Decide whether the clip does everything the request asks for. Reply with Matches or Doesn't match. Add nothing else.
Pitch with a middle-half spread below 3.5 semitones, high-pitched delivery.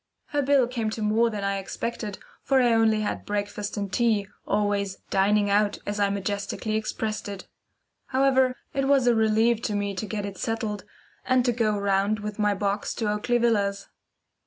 Matches